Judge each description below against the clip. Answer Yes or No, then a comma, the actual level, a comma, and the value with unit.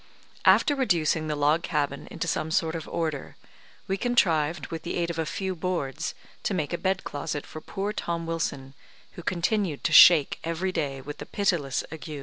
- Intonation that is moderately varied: Yes, average, 3.3 semitones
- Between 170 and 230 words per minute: Yes, average, 185 wpm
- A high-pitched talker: No, medium, 165 Hz